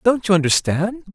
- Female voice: No, male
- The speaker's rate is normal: Yes, average, 155 wpm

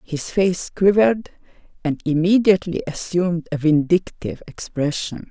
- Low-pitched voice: No, medium, 175 Hz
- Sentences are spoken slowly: Yes, slow, 100 wpm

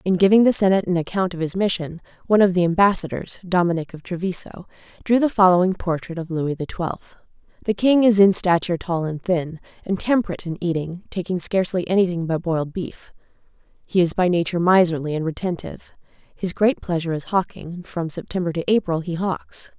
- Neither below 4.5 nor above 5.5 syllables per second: No, 5.9 syllables/s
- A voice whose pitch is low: No, medium, 180 Hz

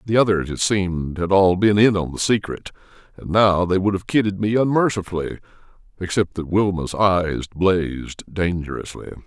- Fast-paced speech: No, average, 160 wpm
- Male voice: Yes, male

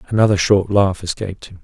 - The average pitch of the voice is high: No, low, 100 Hz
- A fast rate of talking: No, average, 185 wpm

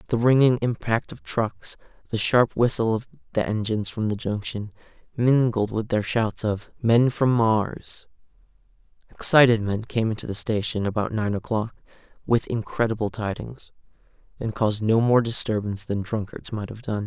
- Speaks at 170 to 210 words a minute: No, average, 155 wpm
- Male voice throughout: Yes, male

